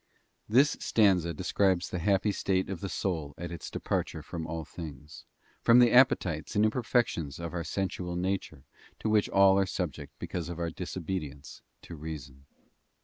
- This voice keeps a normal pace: Yes, average, 165 wpm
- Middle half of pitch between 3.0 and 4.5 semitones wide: Yes, average, 3.4 semitones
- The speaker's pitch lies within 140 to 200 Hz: No, very low, 90 Hz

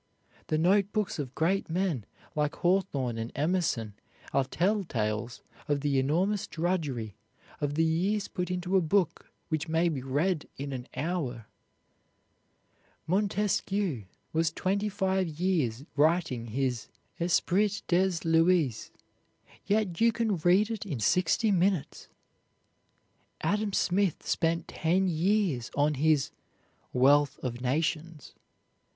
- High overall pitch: No, medium, 165 Hz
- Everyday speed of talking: No, slow, 120 wpm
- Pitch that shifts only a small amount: No, average, 5.2 semitones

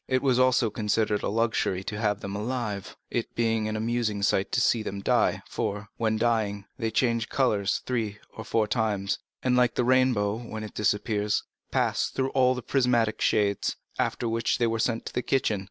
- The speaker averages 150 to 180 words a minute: No, average, 190 wpm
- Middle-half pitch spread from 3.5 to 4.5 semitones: No, average, 2.7 semitones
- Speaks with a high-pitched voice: No, low, 110 Hz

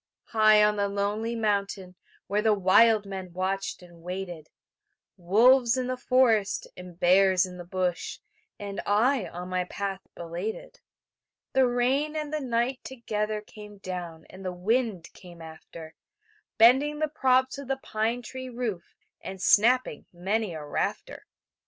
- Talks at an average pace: Yes, average, 145 wpm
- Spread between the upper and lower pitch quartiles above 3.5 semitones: Yes, average, 5.0 semitones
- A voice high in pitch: Yes, high, 205 Hz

